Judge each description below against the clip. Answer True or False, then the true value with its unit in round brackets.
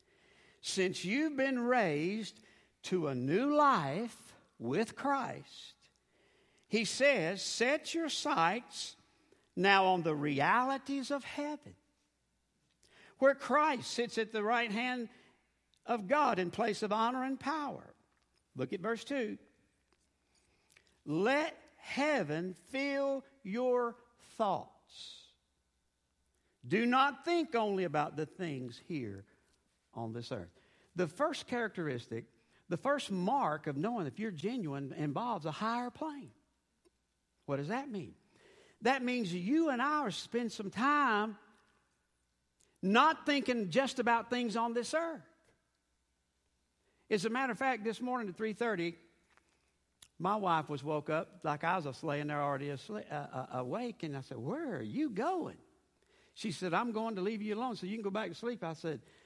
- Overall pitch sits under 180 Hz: False (215 Hz)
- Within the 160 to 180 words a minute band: False (140 wpm)